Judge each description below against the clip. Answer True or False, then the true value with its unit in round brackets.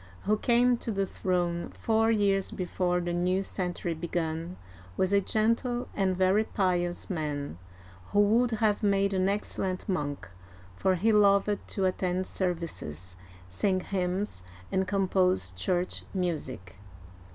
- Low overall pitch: False (185 Hz)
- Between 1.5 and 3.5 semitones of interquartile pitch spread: True (2.6 semitones)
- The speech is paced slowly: True (130 wpm)